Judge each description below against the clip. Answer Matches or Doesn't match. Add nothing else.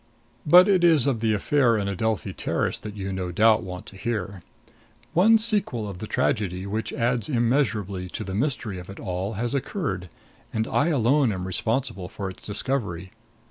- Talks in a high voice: Doesn't match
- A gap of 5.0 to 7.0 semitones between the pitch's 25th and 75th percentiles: Matches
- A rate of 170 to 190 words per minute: Matches